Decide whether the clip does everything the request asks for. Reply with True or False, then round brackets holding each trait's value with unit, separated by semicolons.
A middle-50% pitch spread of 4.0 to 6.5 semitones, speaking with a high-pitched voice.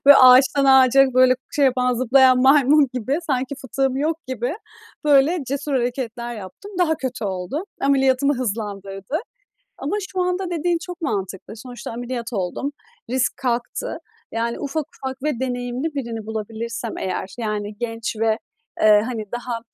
False (3.4 semitones; 255 Hz)